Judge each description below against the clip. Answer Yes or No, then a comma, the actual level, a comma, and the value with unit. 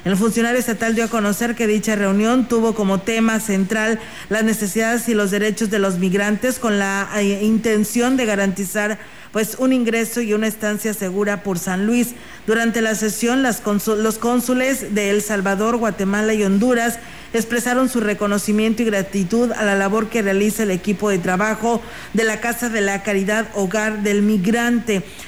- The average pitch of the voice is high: Yes, high, 215 Hz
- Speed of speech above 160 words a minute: Yes, average, 170 wpm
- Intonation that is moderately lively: No, narrow, 2.0 semitones